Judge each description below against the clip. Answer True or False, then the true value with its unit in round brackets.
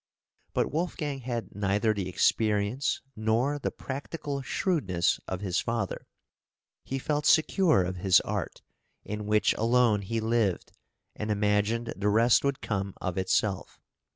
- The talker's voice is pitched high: False (110 Hz)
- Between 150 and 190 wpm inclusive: False (135 wpm)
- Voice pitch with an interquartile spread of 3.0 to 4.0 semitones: False (4.7 semitones)